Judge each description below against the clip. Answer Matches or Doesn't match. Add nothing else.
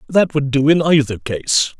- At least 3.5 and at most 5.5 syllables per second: Matches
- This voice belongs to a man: Matches